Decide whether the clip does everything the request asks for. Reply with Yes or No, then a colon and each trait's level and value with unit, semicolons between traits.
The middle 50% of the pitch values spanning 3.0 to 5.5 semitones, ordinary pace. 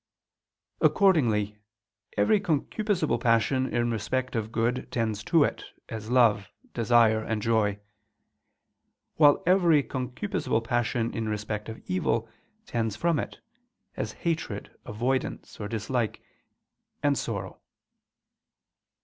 No: average, 3.8 semitones; slow, 105 wpm